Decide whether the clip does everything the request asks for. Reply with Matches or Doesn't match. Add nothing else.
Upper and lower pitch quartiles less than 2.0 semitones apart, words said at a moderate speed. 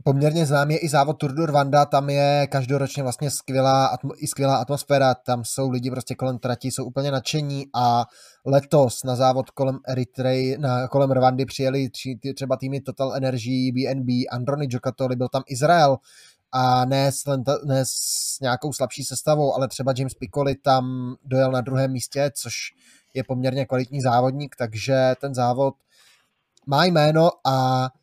Matches